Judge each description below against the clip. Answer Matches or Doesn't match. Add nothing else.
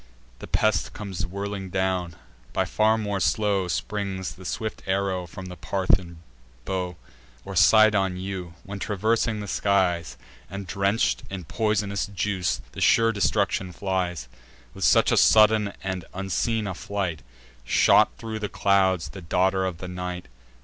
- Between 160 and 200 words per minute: Doesn't match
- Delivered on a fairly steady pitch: Matches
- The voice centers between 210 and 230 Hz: Doesn't match